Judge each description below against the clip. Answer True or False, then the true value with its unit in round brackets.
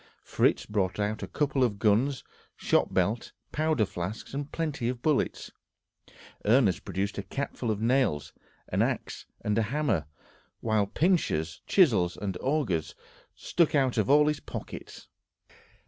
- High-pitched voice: False (115 Hz)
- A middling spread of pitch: False (6.0 semitones)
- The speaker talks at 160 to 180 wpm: False (145 wpm)